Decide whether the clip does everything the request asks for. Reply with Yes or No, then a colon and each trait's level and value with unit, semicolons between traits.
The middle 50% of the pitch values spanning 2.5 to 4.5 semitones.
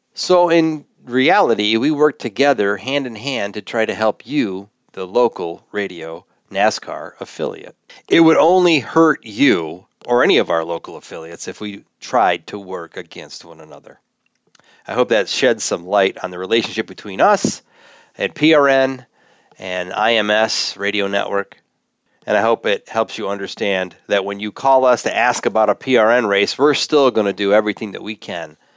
No: average, 5.2 semitones